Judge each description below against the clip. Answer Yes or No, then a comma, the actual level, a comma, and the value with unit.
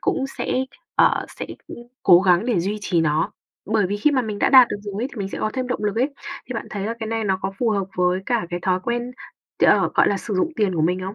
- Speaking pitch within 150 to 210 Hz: Yes, high, 205 Hz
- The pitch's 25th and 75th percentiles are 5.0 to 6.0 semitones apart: No, average, 4.3 semitones